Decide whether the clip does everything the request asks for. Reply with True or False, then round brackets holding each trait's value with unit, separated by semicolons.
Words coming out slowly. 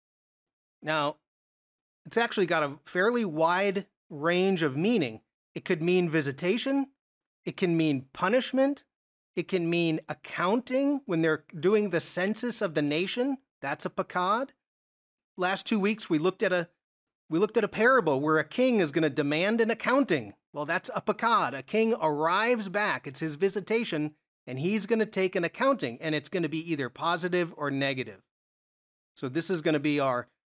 False (175 wpm)